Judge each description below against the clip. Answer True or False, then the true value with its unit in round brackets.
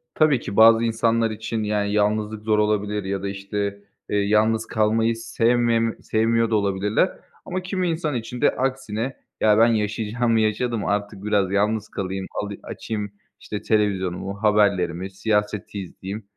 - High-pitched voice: False (105 Hz)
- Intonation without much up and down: True (1.9 semitones)